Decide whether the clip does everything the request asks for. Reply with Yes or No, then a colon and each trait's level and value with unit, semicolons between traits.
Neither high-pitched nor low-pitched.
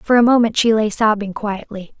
No: high, 215 Hz